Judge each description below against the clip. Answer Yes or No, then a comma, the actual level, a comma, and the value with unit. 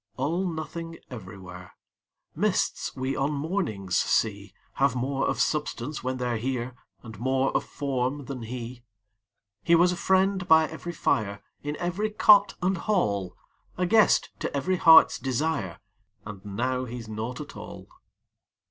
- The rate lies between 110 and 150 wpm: Yes, average, 145 wpm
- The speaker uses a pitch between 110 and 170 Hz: Yes, low, 135 Hz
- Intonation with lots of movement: Yes, wide, 6.2 semitones